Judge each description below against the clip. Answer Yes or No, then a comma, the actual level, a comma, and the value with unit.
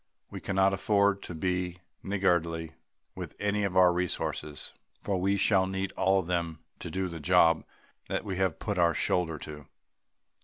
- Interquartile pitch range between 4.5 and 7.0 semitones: No, narrow, 2.4 semitones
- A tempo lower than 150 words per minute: No, average, 165 wpm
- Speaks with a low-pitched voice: Yes, very low, 90 Hz